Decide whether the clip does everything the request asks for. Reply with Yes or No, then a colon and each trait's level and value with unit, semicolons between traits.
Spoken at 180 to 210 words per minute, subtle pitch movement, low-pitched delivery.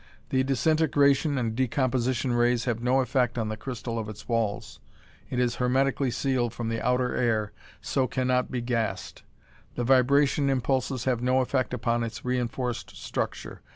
No: average, 160 wpm; narrow, 2.0 semitones; low, 125 Hz